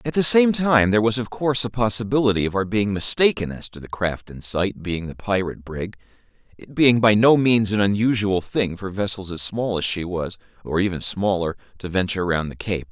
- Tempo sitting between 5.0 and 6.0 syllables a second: Yes, 5.5 syllables/s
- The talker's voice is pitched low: Yes, low, 105 Hz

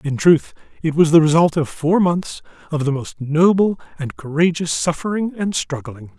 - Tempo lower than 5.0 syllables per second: Yes, 4.7 syllables/s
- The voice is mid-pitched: Yes, medium, 160 Hz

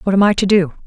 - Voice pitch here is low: No, high, 190 Hz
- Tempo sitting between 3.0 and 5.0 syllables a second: No, 7.5 syllables/s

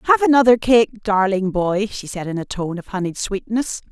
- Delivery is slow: No, average, 200 wpm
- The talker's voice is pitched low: No, high, 210 Hz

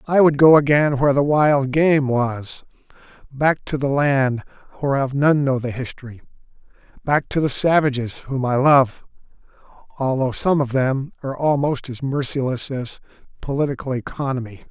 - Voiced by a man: Yes, male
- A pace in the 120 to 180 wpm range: Yes, average, 145 wpm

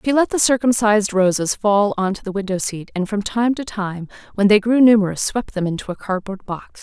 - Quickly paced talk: Yes, fast, 230 wpm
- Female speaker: Yes, female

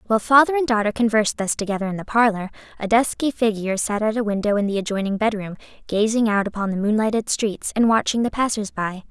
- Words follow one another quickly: Yes, fast, 210 wpm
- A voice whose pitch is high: Yes, high, 215 Hz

